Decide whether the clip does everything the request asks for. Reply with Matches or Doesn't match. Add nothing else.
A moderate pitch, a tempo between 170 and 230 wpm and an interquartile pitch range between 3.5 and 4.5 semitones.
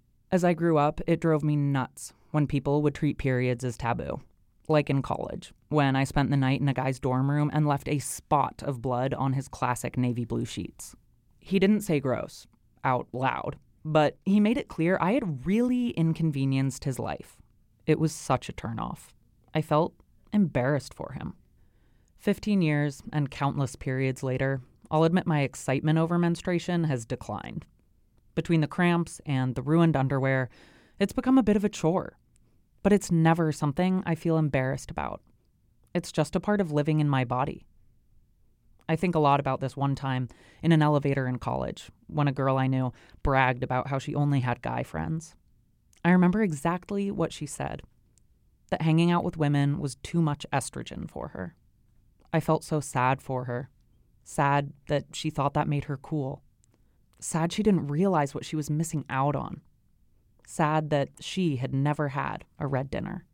Matches